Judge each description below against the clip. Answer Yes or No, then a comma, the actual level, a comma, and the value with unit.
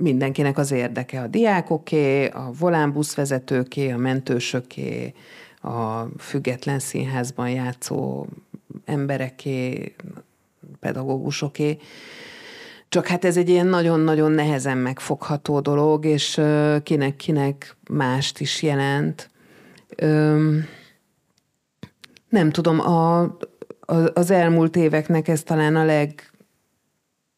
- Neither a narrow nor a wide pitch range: Yes, average, 3.3 semitones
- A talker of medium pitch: Yes, medium, 150 Hz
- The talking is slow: Yes, slow, 85 wpm